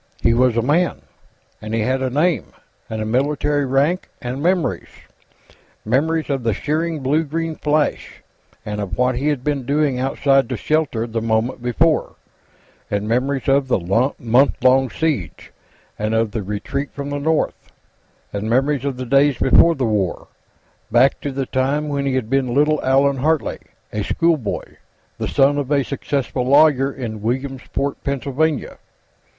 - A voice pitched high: No, low, 135 Hz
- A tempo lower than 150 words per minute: No, average, 160 wpm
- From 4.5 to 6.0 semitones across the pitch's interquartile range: No, average, 3.3 semitones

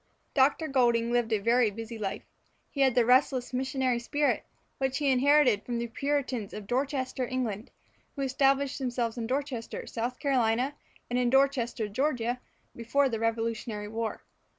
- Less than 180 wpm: Yes, average, 150 wpm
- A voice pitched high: Yes, very high, 250 Hz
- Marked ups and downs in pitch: No, average, 2.8 semitones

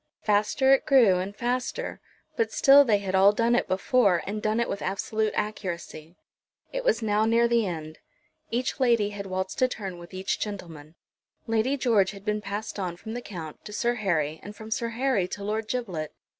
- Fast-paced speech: No, average, 195 wpm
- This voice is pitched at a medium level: No, high, 210 Hz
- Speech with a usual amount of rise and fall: Yes, average, 3.9 semitones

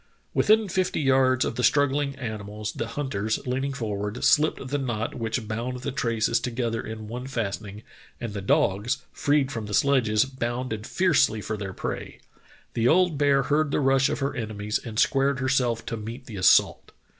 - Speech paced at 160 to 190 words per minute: Yes, average, 175 wpm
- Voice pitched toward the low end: Yes, low, 125 Hz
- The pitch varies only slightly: No, average, 4.0 semitones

